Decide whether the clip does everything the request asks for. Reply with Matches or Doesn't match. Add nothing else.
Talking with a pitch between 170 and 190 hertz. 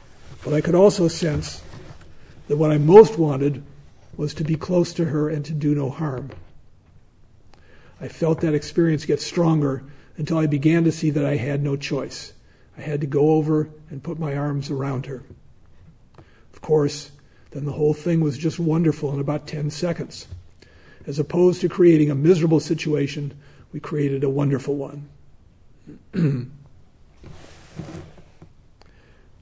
Doesn't match